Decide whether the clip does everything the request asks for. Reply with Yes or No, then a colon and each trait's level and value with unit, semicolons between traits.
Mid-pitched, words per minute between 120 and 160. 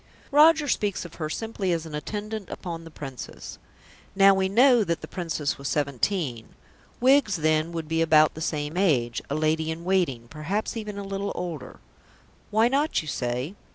No: medium, 170 Hz; average, 175 wpm